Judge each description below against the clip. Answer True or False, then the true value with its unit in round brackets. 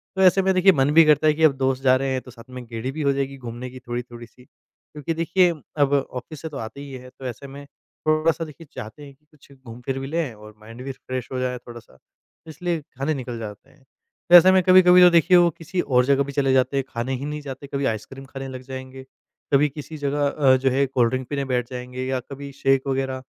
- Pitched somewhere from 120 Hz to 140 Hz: True (135 Hz)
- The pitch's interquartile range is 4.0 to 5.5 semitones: False (2.8 semitones)